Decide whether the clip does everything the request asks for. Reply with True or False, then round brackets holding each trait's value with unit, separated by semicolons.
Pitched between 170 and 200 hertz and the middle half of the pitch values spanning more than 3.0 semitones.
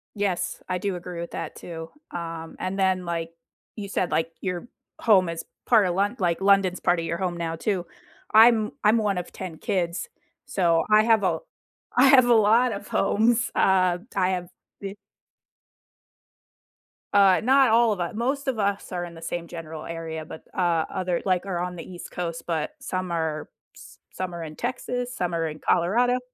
True (185 Hz; 3.7 semitones)